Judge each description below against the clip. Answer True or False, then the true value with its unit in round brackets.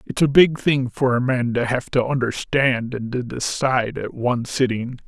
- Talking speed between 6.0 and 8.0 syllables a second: False (4.7 syllables/s)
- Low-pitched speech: True (125 Hz)